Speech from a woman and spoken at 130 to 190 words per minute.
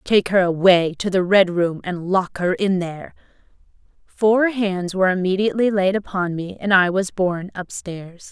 Yes: female; average, 175 wpm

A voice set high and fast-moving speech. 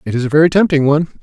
No: medium, 150 Hz; fast, 295 wpm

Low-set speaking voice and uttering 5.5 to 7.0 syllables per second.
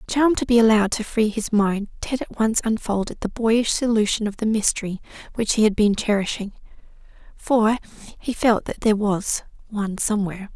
No: high, 215 Hz; 5.6 syllables/s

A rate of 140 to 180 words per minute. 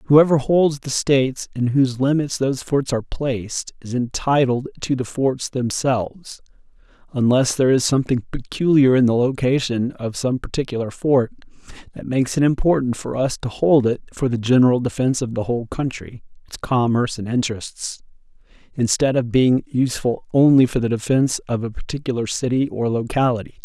Yes: average, 160 wpm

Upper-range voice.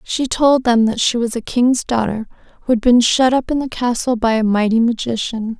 Yes: high, 235 Hz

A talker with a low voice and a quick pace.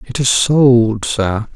No: low, 120 Hz; average, 155 wpm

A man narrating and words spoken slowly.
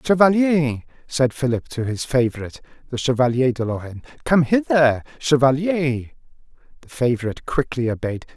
Yes: male; slow, 120 wpm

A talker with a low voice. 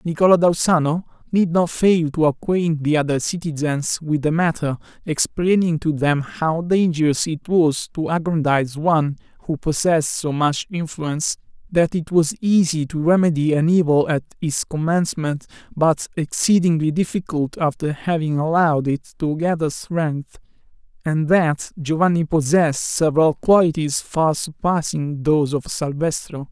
No: medium, 160 Hz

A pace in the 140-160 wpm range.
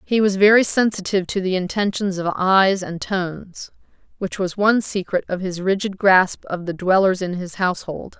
No: average, 185 wpm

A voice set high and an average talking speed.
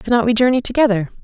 Yes: high, 235 Hz; average, 195 wpm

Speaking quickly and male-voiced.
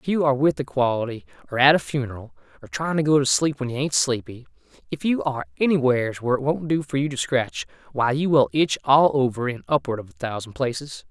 Yes: fast, 240 wpm; male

